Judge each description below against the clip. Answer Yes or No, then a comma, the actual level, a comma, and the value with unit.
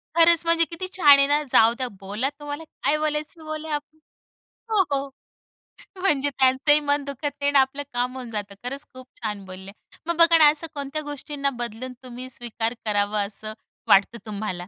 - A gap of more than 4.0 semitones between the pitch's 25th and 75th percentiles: Yes, average, 4.6 semitones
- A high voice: Yes, very high, 275 Hz